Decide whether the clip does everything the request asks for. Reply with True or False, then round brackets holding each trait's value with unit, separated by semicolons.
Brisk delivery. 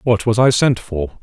True (245 wpm)